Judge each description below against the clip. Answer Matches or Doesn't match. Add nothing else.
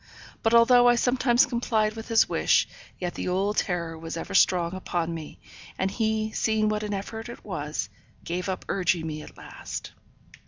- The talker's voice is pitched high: Matches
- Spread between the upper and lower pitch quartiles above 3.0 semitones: Matches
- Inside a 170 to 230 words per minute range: Matches